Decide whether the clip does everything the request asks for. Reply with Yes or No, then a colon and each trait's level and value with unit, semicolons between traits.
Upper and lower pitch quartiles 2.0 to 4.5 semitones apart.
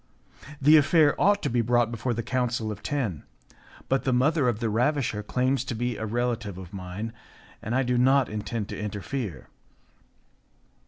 Yes: average, 3.6 semitones